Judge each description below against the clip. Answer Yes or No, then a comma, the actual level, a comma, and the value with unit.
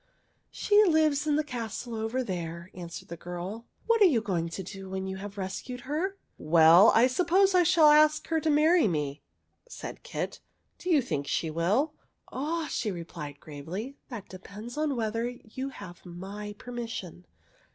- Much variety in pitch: Yes, wide, 8.9 semitones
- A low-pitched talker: No, high, 225 Hz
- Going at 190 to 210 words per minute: Yes, average, 195 wpm